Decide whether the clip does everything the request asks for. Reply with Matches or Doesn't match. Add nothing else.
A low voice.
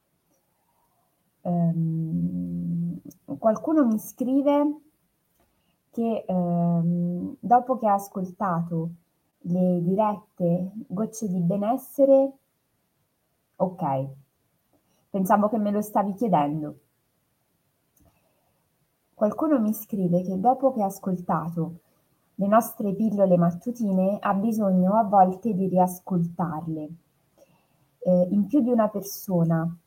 Doesn't match